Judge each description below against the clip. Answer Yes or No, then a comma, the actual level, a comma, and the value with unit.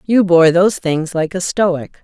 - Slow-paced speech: No, fast, 205 wpm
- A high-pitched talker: No, medium, 175 Hz